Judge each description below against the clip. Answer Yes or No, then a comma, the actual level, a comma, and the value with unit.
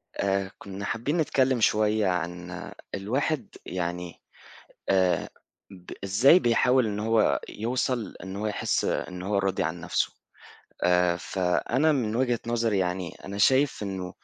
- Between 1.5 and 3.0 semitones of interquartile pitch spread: No, average, 4.6 semitones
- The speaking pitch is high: No, low, 100 Hz